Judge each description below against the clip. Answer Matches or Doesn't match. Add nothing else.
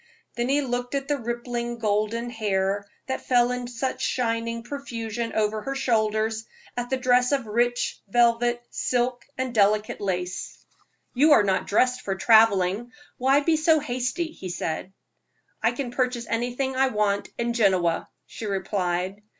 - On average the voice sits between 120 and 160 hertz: Doesn't match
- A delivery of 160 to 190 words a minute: Doesn't match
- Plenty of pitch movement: Doesn't match